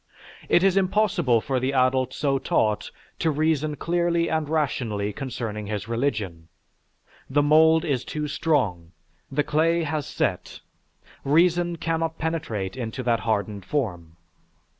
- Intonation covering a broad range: Yes, wide, 6.3 semitones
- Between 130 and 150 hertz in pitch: Yes, medium, 140 Hz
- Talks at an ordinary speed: No, slow, 130 wpm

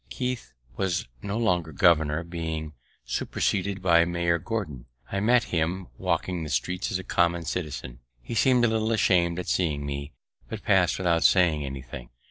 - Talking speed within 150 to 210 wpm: Yes, average, 160 wpm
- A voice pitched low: Yes, very low, 85 Hz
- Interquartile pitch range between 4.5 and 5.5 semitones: No, average, 3.7 semitones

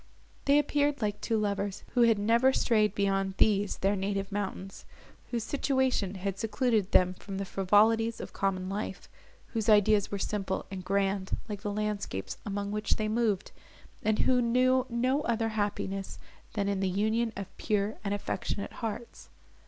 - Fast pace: No, average, 160 wpm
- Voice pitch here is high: Yes, high, 210 Hz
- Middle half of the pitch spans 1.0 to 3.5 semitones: Yes, narrow, 2.6 semitones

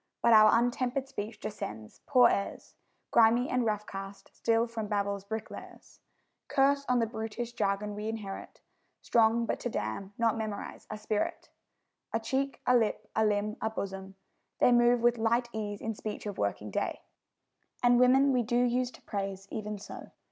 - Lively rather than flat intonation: No, average, 2.7 semitones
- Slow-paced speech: No, average, 170 wpm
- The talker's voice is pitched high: Yes, high, 220 Hz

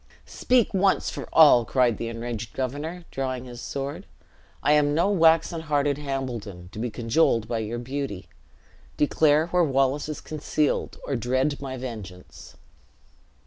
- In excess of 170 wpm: No, average, 145 wpm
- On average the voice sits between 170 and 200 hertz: No, low, 135 Hz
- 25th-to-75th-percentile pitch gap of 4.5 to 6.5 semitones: No, average, 4.0 semitones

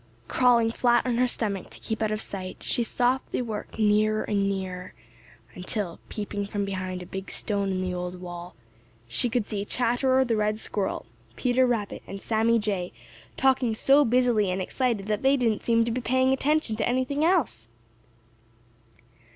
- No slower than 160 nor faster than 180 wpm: Yes, average, 175 wpm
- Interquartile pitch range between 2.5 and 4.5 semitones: Yes, average, 3.9 semitones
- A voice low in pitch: No, high, 220 Hz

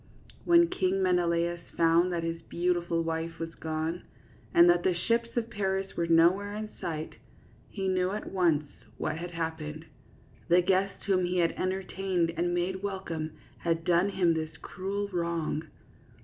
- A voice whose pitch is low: No, medium, 175 Hz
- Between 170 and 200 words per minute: No, average, 160 wpm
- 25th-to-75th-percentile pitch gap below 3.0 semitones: Yes, narrow, 2.4 semitones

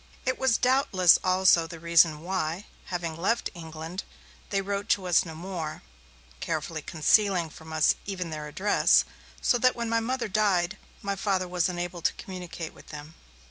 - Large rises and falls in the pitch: No, average, 3.6 semitones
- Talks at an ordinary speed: Yes, average, 165 wpm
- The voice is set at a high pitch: No, medium, 180 Hz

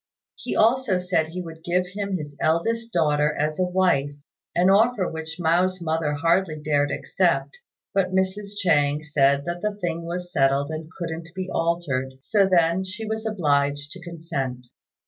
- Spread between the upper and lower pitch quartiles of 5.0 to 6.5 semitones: No, average, 3.8 semitones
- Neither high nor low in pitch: Yes, medium, 170 Hz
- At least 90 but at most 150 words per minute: No, average, 165 wpm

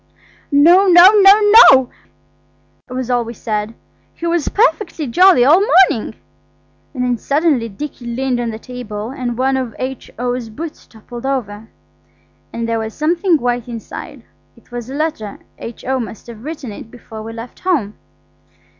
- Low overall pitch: No, very high, 250 Hz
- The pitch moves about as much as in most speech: Yes, average, 5.0 semitones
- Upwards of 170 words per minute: No, average, 150 wpm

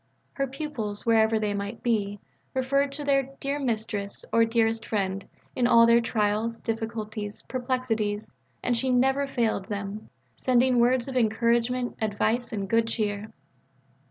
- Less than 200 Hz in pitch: No, high, 230 Hz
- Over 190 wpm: No, average, 140 wpm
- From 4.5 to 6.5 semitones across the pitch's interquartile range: No, average, 2.9 semitones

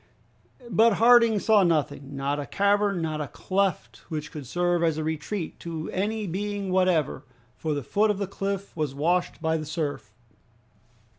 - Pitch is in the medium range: Yes, medium, 175 Hz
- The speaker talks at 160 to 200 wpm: Yes, average, 165 wpm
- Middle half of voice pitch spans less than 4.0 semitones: No, average, 4.6 semitones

